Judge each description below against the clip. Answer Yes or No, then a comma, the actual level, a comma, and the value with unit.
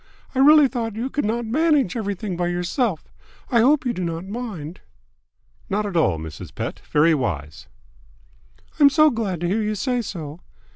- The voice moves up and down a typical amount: No, wide, 6.6 semitones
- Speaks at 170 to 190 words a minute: Yes, average, 175 wpm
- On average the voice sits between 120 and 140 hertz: No, high, 210 Hz